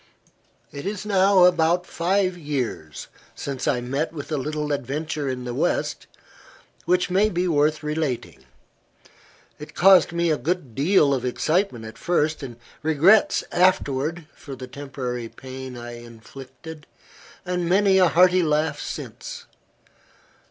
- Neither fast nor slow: No, slow, 130 wpm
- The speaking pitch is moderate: Yes, medium, 155 Hz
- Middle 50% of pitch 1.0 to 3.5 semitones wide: No, average, 4.9 semitones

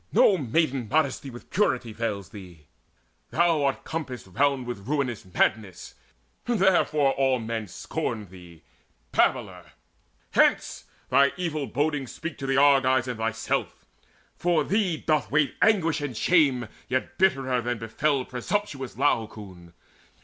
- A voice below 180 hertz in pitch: Yes, low, 135 Hz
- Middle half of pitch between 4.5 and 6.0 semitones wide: Yes, average, 5.2 semitones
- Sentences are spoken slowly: Yes, slow, 130 wpm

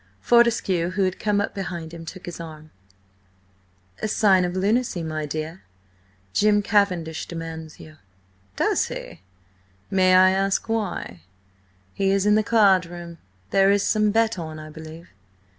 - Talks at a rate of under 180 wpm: Yes, average, 150 wpm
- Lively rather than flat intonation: No, average, 3.8 semitones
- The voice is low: No, medium, 185 Hz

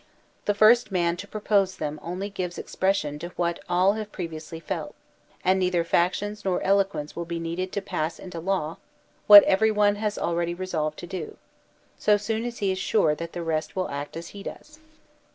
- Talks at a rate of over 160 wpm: Yes, average, 190 wpm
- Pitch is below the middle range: No, medium, 185 Hz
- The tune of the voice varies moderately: Yes, average, 3.3 semitones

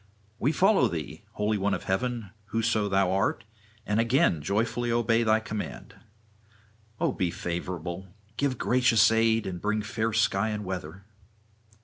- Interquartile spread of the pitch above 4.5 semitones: No, average, 3.1 semitones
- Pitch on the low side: Yes, low, 110 Hz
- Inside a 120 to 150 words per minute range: Yes, average, 140 wpm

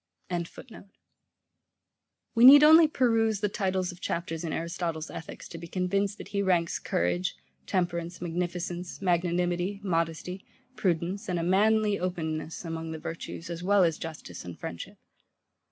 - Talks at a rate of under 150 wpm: Yes, average, 140 wpm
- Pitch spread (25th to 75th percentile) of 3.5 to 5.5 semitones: No, average, 3.0 semitones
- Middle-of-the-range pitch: Yes, medium, 175 Hz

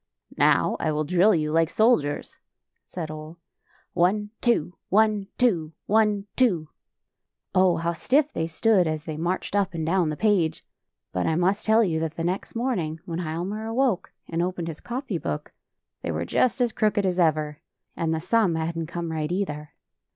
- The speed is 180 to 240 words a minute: Yes, average, 185 wpm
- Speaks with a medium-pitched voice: Yes, medium, 175 Hz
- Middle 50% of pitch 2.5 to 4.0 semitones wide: No, average, 4.6 semitones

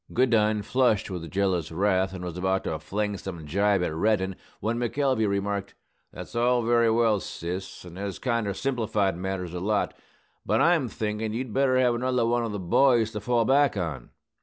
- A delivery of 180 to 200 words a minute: Yes, average, 185 wpm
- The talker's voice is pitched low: Yes, low, 105 Hz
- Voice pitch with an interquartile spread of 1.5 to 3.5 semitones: No, average, 3.9 semitones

